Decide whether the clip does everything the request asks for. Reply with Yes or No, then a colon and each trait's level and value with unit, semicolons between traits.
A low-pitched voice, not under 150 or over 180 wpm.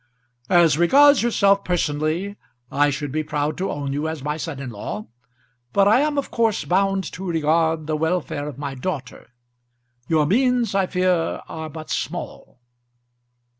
No: medium, 160 Hz; average, 160 wpm